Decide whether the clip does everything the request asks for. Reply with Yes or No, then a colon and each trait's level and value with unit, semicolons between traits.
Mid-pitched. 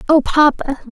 No: very high, 280 Hz